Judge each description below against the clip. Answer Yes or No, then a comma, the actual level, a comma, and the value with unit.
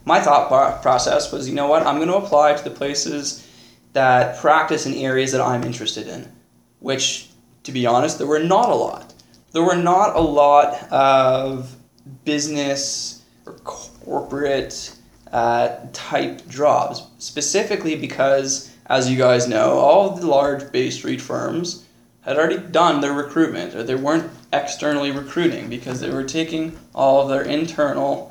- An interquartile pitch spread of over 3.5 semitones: No, average, 3.2 semitones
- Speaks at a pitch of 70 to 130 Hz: No, medium, 140 Hz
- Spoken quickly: No, average, 155 wpm